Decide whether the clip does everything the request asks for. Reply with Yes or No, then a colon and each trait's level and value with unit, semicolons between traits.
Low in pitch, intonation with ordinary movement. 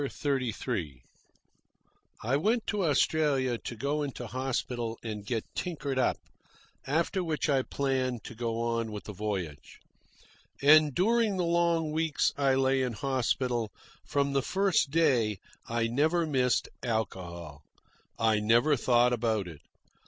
Yes: low, 130 Hz; average, 4.8 semitones